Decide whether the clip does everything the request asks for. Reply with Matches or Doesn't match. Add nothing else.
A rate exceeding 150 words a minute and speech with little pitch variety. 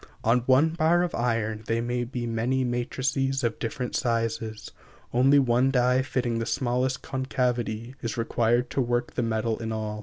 Matches